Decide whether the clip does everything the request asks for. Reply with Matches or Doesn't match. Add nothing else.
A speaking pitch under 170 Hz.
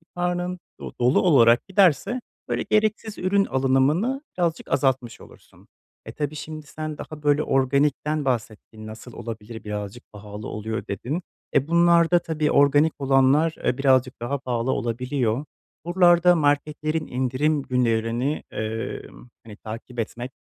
Matches